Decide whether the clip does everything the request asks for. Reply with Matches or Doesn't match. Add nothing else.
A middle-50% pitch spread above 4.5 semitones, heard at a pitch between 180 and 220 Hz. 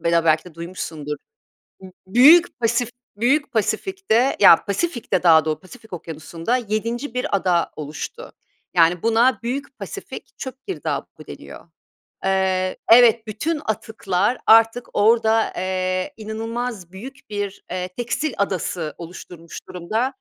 Matches